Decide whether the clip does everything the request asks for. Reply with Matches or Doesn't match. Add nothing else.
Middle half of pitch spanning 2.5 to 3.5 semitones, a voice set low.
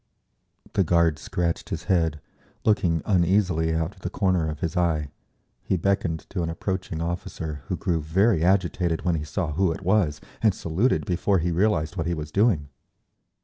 Matches